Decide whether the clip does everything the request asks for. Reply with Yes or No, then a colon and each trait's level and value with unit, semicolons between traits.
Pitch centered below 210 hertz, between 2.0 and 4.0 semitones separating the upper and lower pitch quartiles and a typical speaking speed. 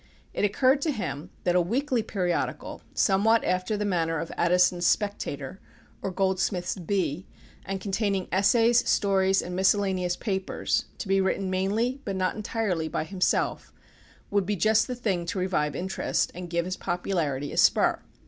Yes: high, 190 Hz; narrow, 2.5 semitones; average, 160 wpm